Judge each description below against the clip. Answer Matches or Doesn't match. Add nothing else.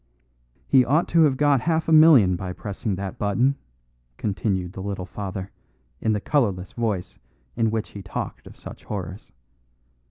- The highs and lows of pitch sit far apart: Matches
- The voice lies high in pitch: Doesn't match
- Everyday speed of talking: Matches